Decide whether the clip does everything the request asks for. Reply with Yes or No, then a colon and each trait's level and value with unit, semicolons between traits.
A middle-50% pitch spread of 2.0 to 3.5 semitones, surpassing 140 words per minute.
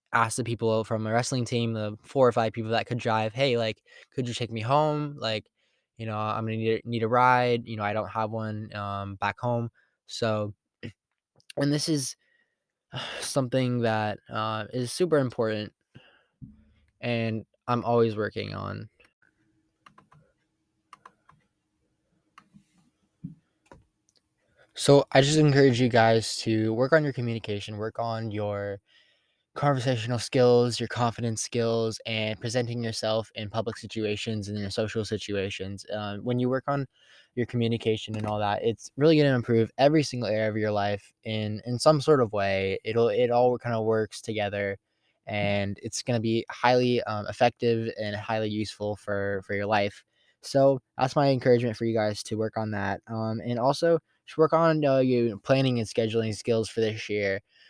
Yes: narrow, 2.5 semitones; average, 165 wpm